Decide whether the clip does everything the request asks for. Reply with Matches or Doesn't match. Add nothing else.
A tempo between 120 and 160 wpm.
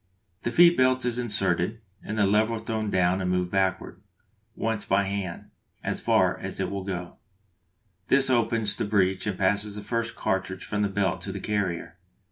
Doesn't match